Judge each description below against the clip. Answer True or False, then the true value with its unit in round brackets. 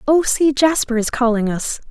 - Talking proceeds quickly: False (190 wpm)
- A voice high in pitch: True (255 Hz)